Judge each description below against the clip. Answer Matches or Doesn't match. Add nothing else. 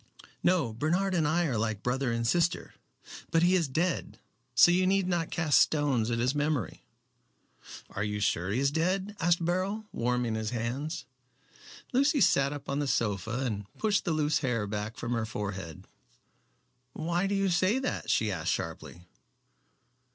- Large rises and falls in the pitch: Matches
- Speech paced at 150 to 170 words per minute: Matches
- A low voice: Doesn't match